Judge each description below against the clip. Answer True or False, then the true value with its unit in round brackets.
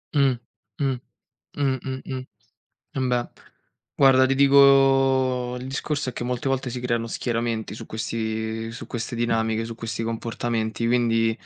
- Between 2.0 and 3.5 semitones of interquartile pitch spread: True (2.6 semitones)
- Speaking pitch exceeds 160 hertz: False (120 Hz)